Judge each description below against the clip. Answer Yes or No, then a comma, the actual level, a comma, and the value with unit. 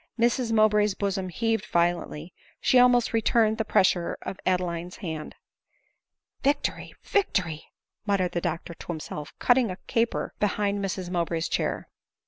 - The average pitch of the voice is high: Yes, high, 195 Hz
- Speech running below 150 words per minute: Yes, average, 140 wpm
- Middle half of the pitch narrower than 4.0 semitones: No, average, 4.6 semitones